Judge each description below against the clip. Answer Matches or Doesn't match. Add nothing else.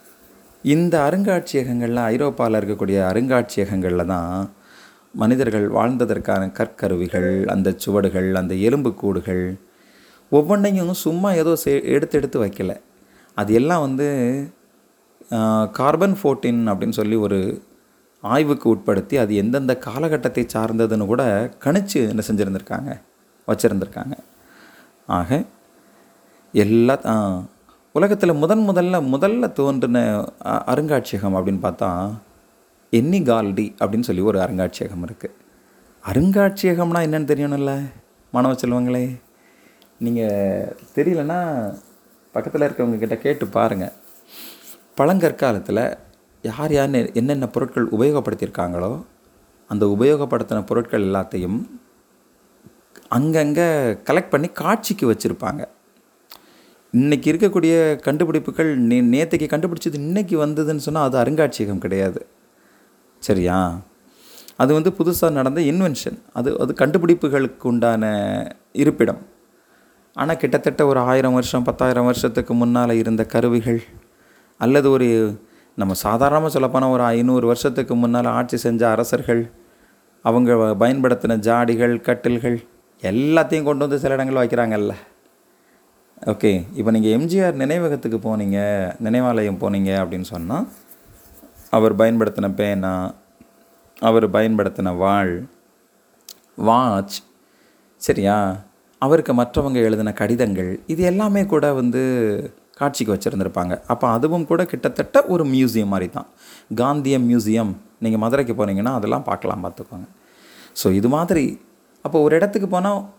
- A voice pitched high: Doesn't match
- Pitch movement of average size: Doesn't match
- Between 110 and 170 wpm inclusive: Doesn't match